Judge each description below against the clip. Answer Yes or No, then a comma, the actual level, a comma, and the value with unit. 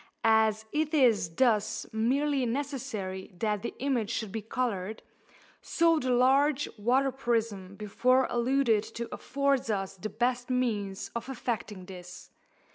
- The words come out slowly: Yes, slow, 130 wpm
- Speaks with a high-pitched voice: Yes, high, 235 Hz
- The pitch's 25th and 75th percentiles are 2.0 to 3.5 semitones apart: No, average, 4.0 semitones